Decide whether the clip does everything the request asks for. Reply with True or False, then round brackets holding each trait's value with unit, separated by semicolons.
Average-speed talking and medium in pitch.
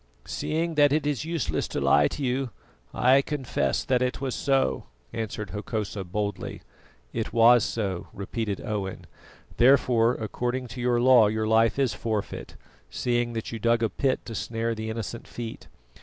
False (160 wpm; 115 Hz)